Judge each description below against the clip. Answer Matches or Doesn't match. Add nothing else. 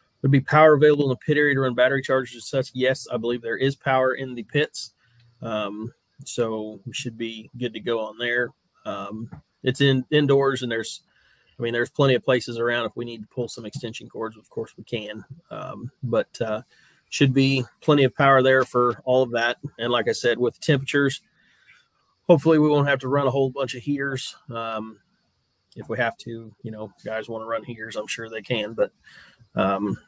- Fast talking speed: Matches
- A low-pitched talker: Matches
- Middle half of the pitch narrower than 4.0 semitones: Matches